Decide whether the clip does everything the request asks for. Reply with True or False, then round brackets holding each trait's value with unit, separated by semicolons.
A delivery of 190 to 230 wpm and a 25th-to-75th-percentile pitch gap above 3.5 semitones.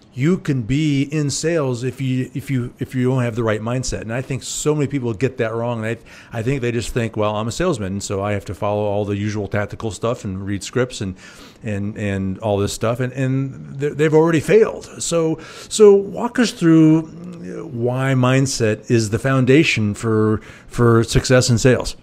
True (205 wpm; 4.6 semitones)